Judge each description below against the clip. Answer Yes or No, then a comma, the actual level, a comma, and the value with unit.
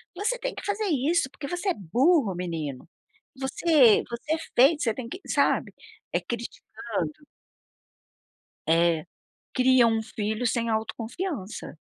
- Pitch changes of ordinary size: No, wide, 6.6 semitones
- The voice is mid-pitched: No, high, 240 Hz